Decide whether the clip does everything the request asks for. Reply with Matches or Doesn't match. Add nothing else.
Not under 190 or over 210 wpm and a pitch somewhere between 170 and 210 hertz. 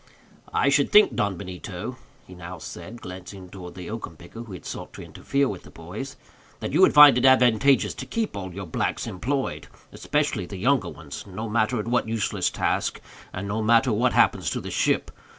Doesn't match